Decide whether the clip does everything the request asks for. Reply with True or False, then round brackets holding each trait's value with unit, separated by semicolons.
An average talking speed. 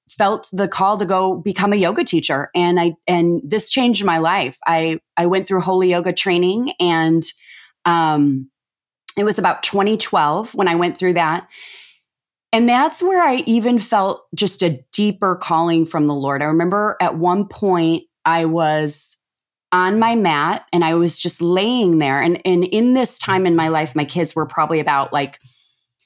True (175 wpm)